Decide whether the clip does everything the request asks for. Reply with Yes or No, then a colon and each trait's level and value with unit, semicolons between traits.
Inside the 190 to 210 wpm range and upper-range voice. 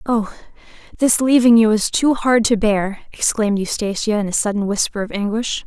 No: average, 180 wpm; high, 215 Hz